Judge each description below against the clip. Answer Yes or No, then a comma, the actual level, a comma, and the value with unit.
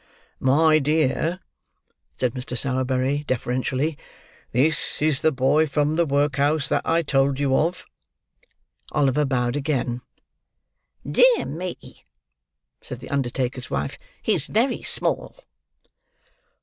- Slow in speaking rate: Yes, slow, 110 wpm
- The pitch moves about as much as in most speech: Yes, average, 3.2 semitones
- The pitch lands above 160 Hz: No, medium, 140 Hz